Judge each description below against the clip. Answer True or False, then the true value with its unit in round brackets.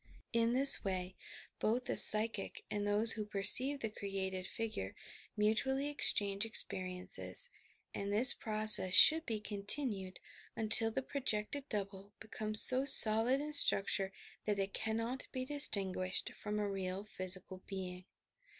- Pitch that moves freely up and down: False (3.1 semitones)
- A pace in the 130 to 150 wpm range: True (135 wpm)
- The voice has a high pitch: True (210 Hz)